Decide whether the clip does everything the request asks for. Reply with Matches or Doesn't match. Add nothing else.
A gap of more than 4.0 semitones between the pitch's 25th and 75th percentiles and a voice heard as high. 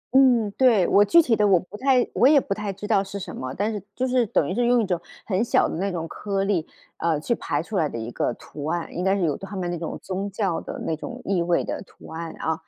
Matches